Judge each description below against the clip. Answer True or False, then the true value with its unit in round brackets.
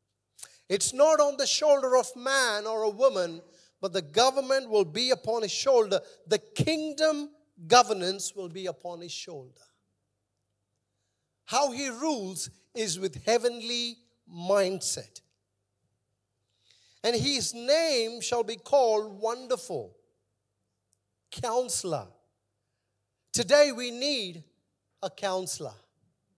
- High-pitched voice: True (195 Hz)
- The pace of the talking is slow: True (105 wpm)